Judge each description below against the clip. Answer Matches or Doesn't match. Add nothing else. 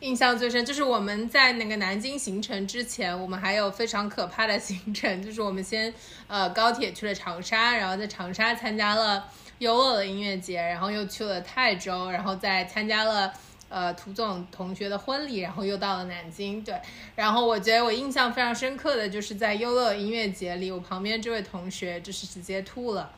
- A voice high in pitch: Matches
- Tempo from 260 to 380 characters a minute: Matches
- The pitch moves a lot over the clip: Doesn't match